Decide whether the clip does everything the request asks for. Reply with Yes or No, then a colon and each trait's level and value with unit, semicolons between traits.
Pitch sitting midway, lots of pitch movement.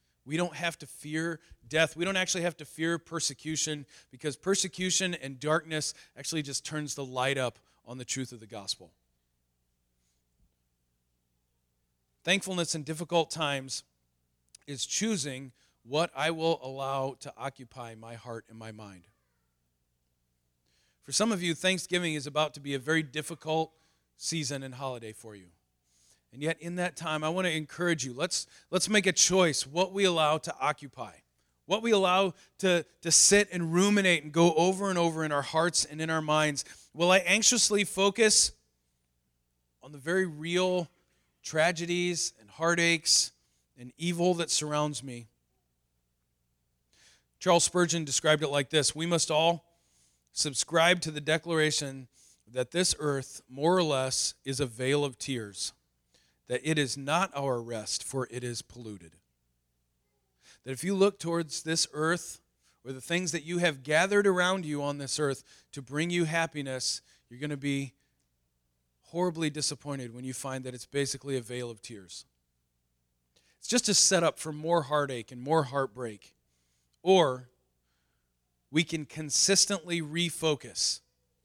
Yes: medium, 145 Hz; wide, 8.9 semitones